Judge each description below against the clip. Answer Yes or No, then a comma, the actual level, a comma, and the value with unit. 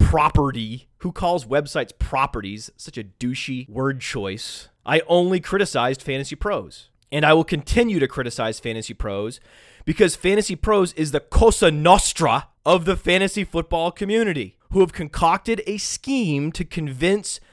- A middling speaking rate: Yes, average, 145 wpm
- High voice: No, medium, 155 Hz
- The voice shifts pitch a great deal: Yes, wide, 6.4 semitones